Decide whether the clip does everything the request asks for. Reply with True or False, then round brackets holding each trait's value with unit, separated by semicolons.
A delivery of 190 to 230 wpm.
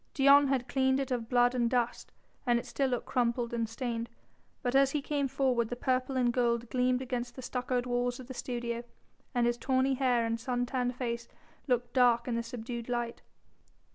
True (200 wpm)